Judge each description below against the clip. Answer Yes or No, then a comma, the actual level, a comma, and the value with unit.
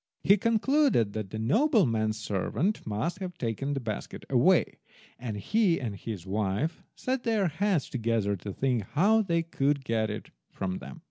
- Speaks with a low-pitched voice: Yes, low, 130 Hz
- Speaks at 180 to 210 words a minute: No, average, 160 wpm